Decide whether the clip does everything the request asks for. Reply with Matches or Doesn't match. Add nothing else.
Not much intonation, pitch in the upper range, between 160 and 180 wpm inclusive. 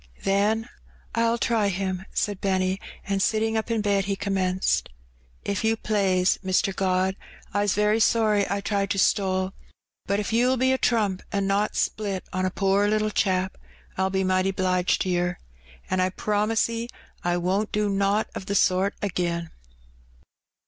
Matches